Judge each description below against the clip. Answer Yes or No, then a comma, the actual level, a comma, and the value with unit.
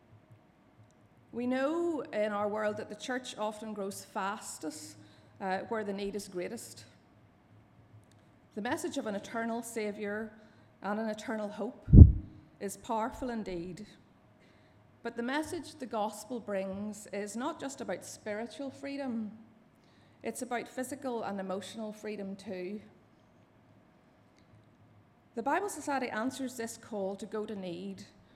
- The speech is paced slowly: Yes, slow, 125 wpm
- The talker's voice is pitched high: Yes, high, 215 Hz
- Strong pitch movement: No, average, 3.7 semitones